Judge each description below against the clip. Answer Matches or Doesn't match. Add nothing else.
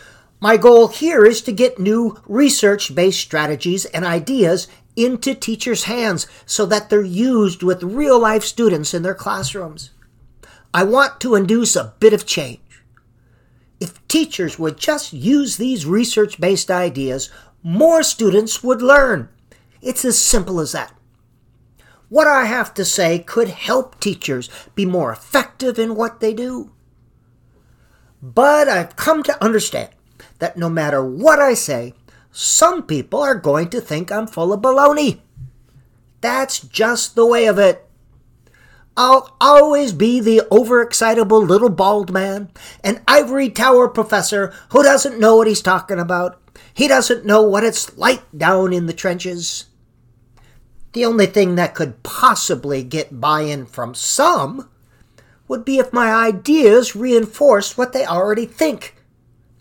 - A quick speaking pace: Doesn't match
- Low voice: Doesn't match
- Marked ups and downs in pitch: Matches